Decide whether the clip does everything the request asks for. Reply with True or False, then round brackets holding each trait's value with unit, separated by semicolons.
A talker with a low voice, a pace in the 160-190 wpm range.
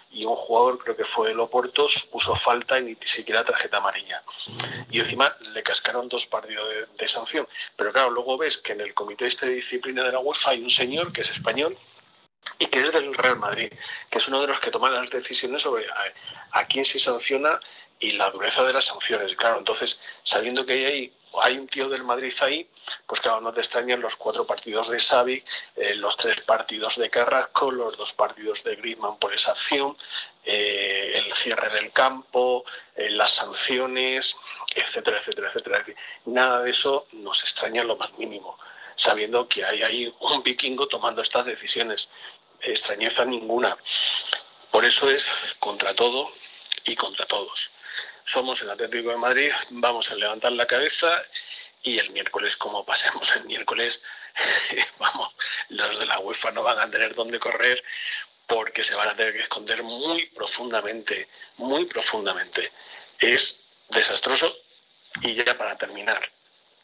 False (360 Hz; 170 wpm)